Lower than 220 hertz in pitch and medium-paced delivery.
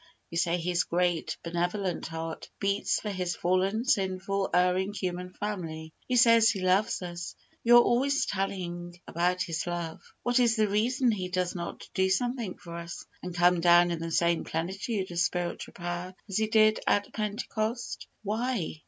Yes: medium, 185 Hz; average, 170 wpm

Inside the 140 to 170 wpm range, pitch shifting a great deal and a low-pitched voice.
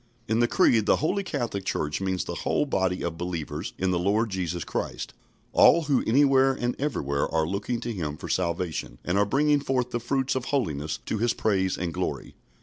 No: average, 200 wpm; wide, 6.8 semitones; low, 100 Hz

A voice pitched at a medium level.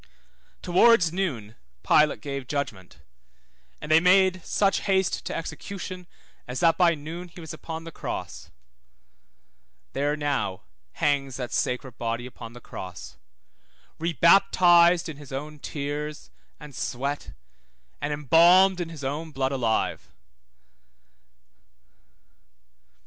Yes: medium, 150 Hz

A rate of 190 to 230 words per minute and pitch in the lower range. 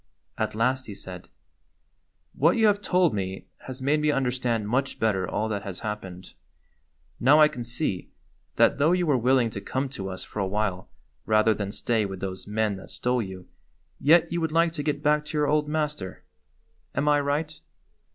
Yes: average, 195 wpm; low, 125 Hz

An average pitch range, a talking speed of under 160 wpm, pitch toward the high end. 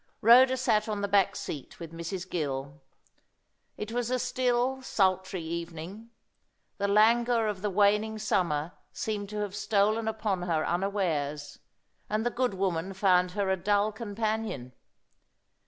Yes: average, 3.6 semitones; average, 140 wpm; high, 200 Hz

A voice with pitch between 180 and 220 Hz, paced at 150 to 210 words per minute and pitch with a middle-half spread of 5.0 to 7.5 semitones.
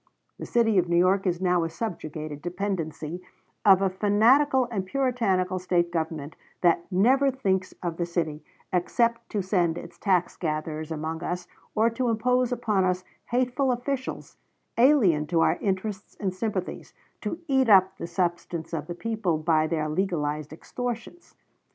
Yes: medium, 185 Hz; average, 155 wpm; average, 5.3 semitones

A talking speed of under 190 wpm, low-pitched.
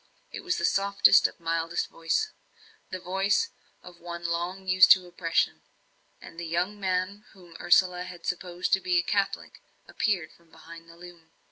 No: average, 160 wpm; medium, 180 Hz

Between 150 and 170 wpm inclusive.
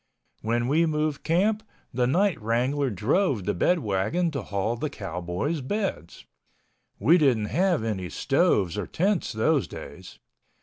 No: slow, 135 wpm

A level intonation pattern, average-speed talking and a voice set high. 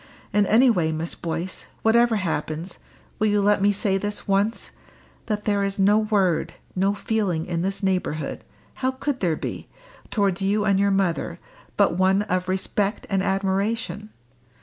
Yes: narrow, 2.0 semitones; average, 160 wpm; high, 195 Hz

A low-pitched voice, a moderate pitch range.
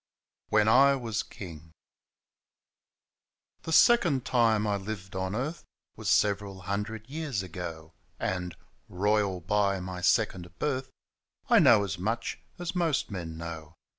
Yes: low, 100 Hz; average, 4.5 semitones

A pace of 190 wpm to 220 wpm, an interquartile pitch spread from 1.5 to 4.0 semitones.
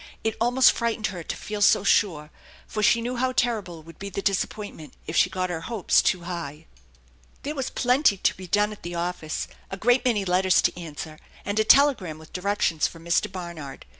No: average, 200 wpm; average, 4.6 semitones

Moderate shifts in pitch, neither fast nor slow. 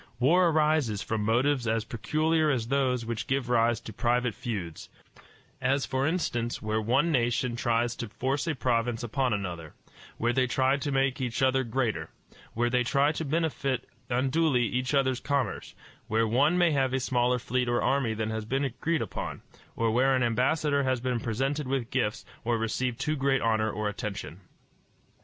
Yes: average, 3.1 semitones; average, 175 wpm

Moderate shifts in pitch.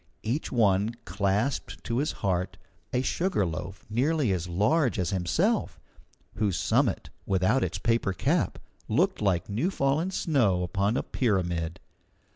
No: wide, 6.2 semitones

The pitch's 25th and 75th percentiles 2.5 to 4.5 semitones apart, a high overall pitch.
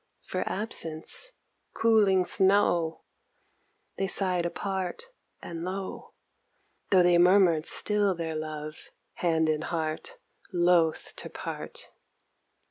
No: average, 3.2 semitones; medium, 180 Hz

